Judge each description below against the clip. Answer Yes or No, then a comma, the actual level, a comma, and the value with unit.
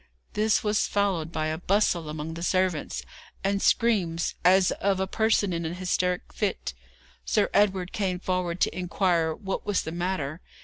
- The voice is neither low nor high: Yes, medium, 180 Hz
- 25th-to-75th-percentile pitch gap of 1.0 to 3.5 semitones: Yes, average, 2.8 semitones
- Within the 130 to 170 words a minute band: Yes, average, 165 wpm